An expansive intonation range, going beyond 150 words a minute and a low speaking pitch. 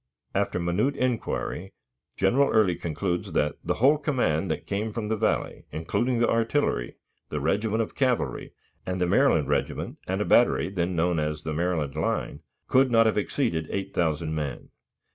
Yes: wide, 6.2 semitones; average, 160 wpm; very low, 95 Hz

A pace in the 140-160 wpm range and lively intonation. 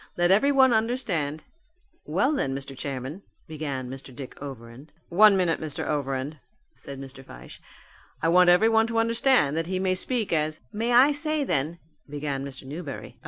No: average, 170 wpm; wide, 8.2 semitones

